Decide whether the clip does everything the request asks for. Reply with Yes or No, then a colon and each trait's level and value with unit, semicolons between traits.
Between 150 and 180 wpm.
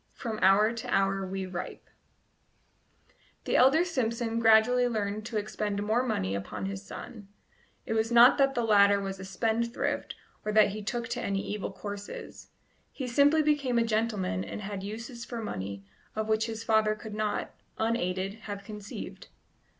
Yes: average, 165 wpm